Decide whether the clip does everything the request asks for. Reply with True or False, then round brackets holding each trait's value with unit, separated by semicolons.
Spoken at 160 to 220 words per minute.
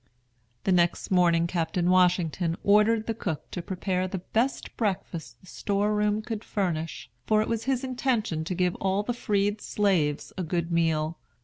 True (170 wpm)